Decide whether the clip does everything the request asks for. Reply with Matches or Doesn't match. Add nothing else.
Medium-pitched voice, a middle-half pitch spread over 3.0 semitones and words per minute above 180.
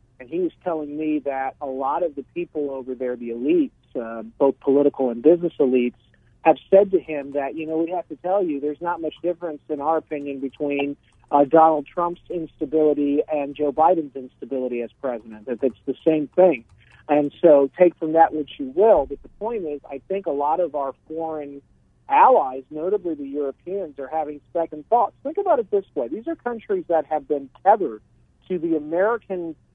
Matches